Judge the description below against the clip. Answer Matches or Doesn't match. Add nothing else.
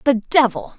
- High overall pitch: Matches